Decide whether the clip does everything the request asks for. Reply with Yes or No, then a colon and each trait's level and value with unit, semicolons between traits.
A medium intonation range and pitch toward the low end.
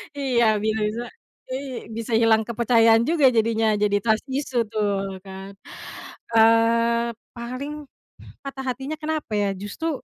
No: average, 3.1 semitones; high, 230 Hz